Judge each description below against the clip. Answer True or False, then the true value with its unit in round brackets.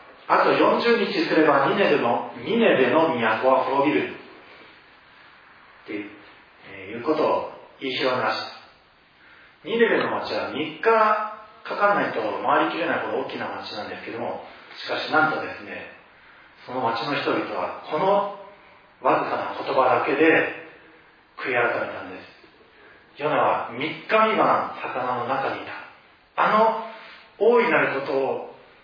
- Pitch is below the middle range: False (220 Hz)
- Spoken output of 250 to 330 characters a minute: True (255 characters per minute)